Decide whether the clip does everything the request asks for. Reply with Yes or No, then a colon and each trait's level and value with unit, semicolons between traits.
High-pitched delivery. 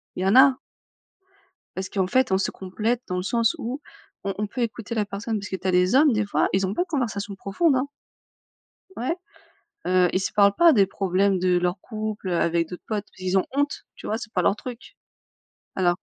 Yes: high, 200 Hz